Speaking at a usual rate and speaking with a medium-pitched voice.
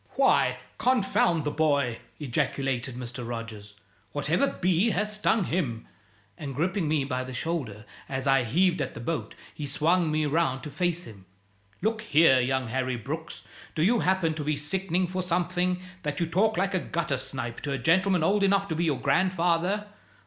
Yes: average, 180 wpm; medium, 160 Hz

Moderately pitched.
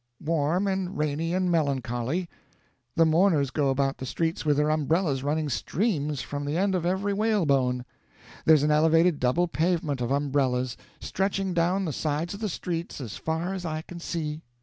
Yes: medium, 160 Hz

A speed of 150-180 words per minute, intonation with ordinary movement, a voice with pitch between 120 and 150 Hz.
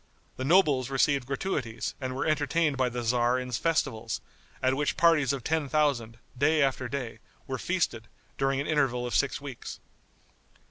Yes: average, 165 wpm; average, 3.0 semitones; low, 135 Hz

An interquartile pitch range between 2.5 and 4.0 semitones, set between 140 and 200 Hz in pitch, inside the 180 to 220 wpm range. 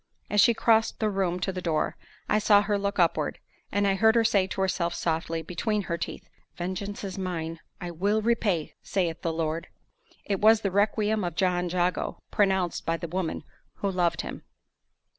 Yes: average, 3.2 semitones; high, 190 Hz; average, 185 wpm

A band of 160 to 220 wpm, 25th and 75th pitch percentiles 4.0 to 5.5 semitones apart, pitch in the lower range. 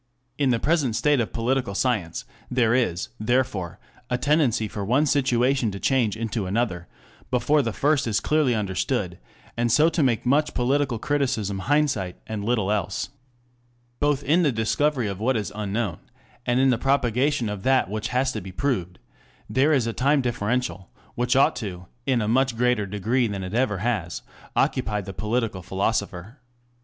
Yes: average, 170 wpm; average, 4.3 semitones; low, 120 Hz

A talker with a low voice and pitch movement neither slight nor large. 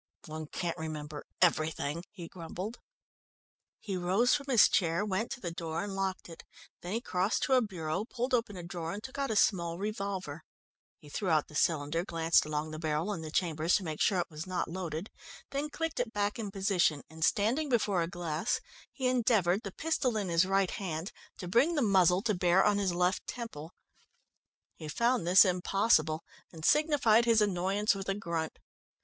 No: medium, 185 Hz; average, 4.4 semitones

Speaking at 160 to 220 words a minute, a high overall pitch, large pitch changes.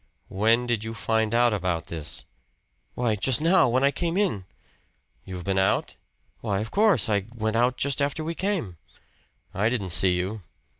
No: average, 170 wpm; low, 115 Hz; wide, 5.8 semitones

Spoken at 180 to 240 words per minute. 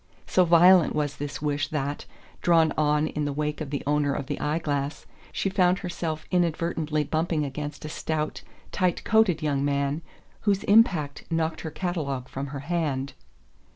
No: average, 165 wpm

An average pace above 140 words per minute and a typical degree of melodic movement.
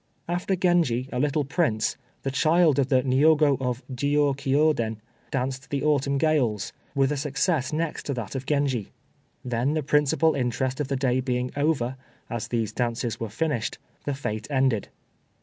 Yes: average, 165 wpm; average, 3.1 semitones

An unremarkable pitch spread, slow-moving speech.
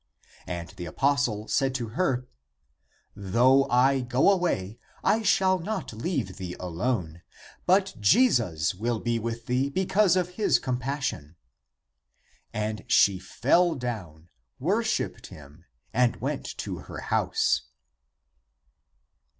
No: wide, 8.4 semitones; slow, 120 wpm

